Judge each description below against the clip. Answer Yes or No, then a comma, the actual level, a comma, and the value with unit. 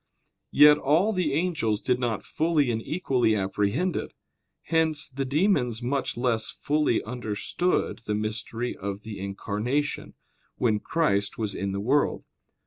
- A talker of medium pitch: No, low, 125 Hz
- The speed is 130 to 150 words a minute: Yes, slow, 135 wpm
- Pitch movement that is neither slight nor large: No, wide, 5.8 semitones